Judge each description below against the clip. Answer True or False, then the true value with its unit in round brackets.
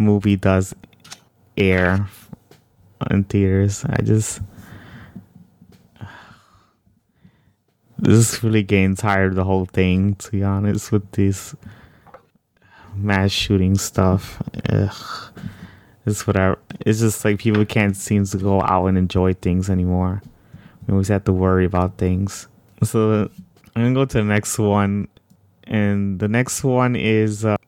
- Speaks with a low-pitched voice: True (100 Hz)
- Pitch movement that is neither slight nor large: False (2.1 semitones)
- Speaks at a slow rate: True (130 wpm)